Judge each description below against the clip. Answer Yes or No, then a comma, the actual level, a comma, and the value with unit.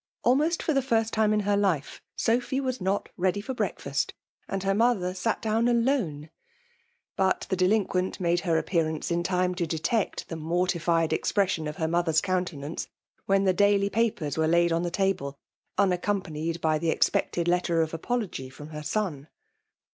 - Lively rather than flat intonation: No, average, 3.9 semitones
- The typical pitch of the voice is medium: Yes, medium, 180 Hz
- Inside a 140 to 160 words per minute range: No, average, 175 wpm